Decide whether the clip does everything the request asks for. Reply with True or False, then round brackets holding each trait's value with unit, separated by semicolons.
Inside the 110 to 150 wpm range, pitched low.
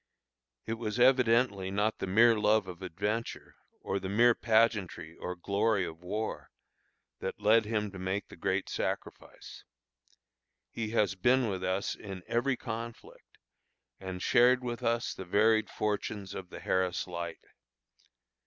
True (145 wpm; 105 Hz)